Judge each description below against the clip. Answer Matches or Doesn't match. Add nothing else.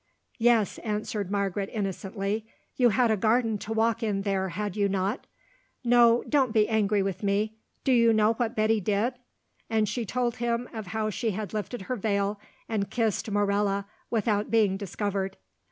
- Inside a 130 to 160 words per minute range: Doesn't match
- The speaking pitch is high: Matches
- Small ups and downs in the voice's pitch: Matches